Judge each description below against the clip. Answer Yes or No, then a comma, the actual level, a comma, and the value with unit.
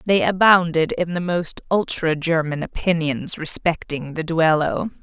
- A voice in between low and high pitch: Yes, medium, 165 Hz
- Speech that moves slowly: Yes, slow, 130 wpm